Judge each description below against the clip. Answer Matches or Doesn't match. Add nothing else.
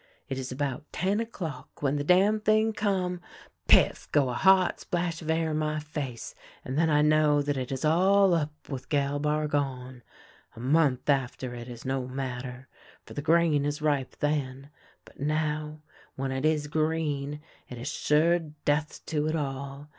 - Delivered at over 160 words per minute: Matches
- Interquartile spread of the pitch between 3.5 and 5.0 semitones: Doesn't match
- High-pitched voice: Doesn't match